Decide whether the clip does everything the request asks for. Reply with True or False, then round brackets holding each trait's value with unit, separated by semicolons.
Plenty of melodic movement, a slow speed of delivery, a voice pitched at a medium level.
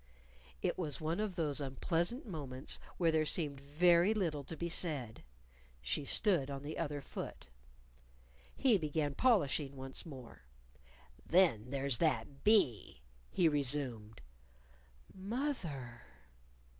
False (4.4 semitones; 120 wpm; 150 Hz)